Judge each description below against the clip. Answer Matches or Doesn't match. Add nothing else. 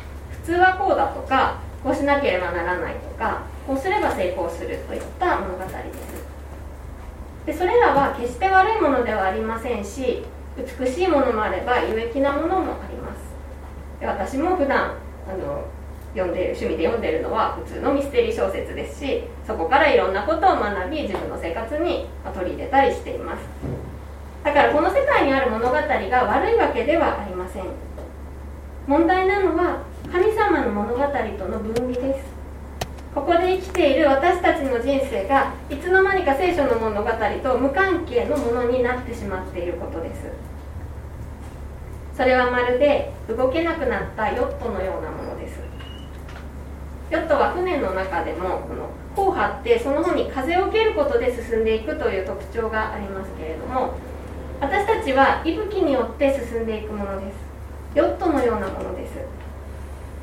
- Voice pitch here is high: Matches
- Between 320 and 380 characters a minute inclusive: Matches